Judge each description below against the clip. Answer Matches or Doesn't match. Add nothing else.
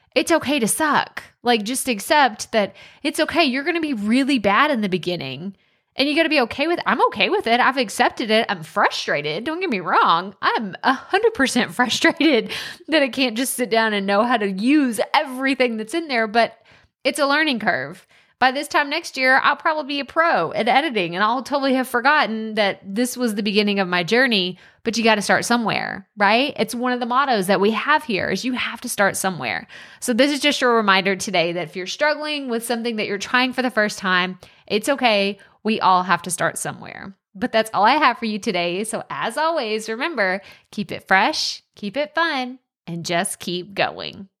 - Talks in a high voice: Matches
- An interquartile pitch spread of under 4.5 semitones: Doesn't match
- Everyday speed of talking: Doesn't match